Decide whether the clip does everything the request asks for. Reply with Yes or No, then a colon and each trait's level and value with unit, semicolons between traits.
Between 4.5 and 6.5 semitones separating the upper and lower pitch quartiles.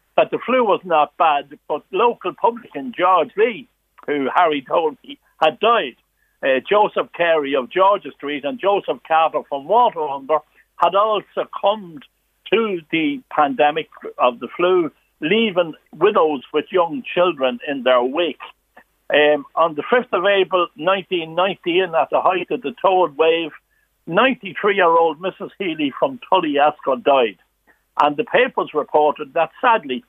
Yes: wide, 5.5 semitones